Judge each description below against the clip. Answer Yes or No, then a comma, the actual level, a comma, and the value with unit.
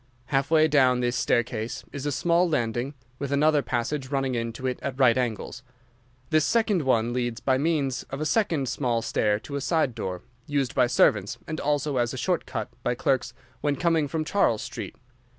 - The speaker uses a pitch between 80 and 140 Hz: Yes, low, 135 Hz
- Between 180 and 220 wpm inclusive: Yes, average, 190 wpm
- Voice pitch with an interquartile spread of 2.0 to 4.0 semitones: Yes, average, 3.7 semitones